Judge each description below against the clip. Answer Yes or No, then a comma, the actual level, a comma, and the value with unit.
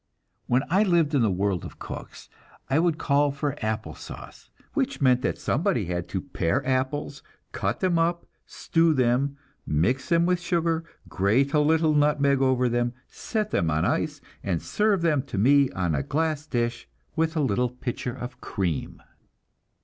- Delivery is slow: No, average, 170 wpm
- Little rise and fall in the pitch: No, wide, 5.4 semitones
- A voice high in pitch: No, medium, 140 Hz